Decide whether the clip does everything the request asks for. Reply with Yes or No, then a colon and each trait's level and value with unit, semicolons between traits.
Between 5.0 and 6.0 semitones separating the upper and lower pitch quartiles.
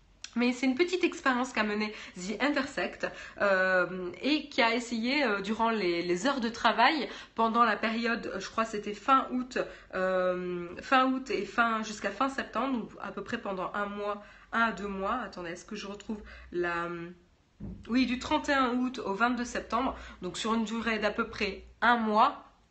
No: average, 4.0 semitones